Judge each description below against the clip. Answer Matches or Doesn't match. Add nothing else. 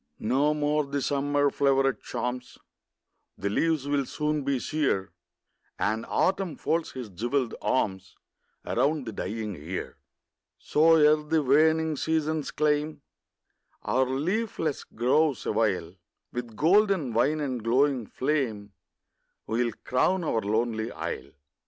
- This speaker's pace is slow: Matches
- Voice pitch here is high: Doesn't match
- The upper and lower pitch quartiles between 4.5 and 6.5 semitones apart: Matches